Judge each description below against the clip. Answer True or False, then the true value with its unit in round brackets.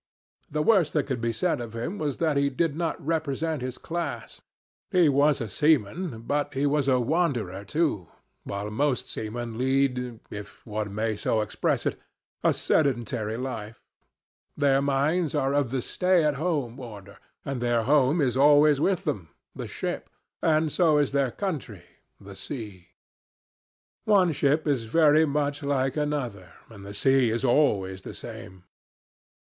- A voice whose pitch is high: False (135 Hz)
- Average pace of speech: True (160 wpm)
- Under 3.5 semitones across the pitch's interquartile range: False (4.8 semitones)